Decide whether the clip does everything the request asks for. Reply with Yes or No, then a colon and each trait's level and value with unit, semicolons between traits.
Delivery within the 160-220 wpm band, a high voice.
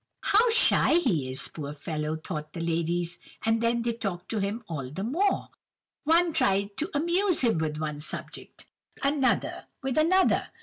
Yes: average, 165 wpm; high, 205 Hz